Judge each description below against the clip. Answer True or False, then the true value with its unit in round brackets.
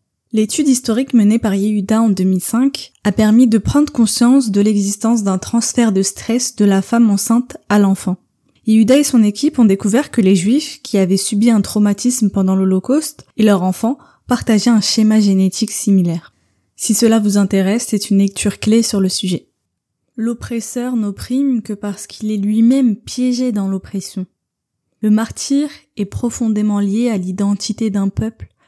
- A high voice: True (215 Hz)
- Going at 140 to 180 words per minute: True (165 wpm)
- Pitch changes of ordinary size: True (3.0 semitones)